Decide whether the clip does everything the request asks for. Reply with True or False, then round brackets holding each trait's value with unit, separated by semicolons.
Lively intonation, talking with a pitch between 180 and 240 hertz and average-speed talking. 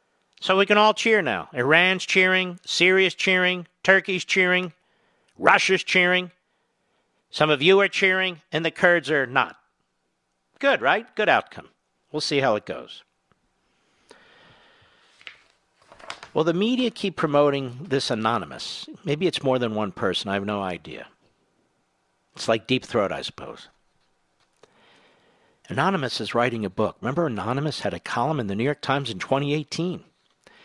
False (6.7 semitones; 155 Hz; 145 wpm)